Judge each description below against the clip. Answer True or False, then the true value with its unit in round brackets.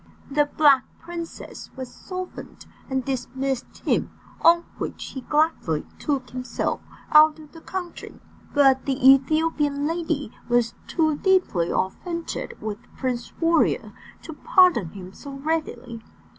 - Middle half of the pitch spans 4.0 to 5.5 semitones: True (4.3 semitones)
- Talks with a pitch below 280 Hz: False (285 Hz)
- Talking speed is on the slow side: True (125 wpm)